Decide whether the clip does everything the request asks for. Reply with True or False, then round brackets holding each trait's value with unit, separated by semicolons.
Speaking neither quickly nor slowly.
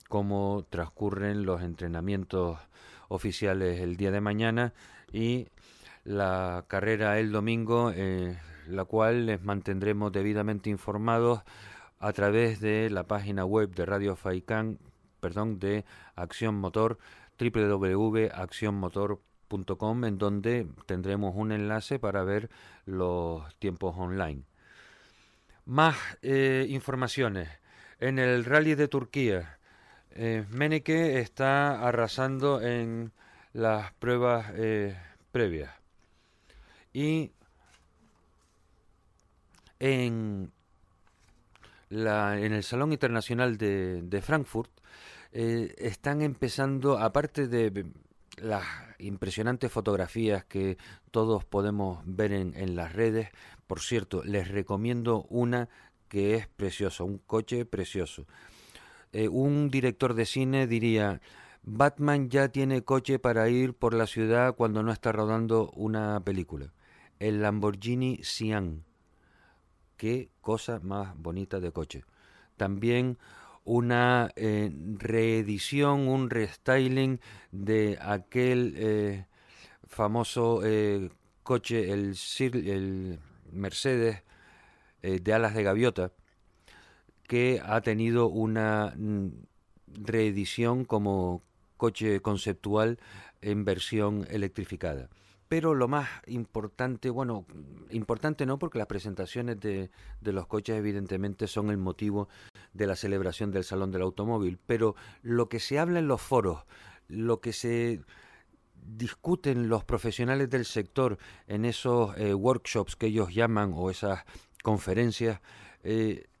False (110 wpm)